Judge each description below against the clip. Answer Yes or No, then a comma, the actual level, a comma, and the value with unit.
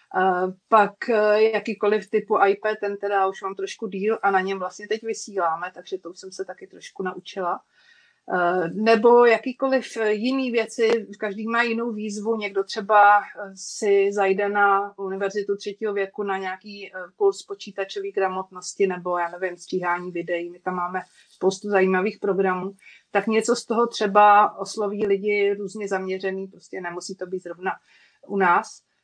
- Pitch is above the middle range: Yes, high, 200 Hz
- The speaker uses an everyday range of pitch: No, narrow, 2.3 semitones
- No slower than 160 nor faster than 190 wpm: No, average, 150 wpm